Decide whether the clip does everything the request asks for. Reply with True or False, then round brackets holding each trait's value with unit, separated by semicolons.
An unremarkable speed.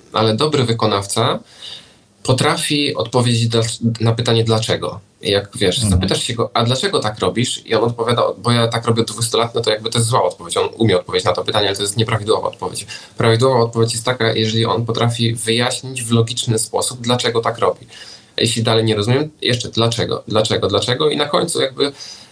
False (195 wpm)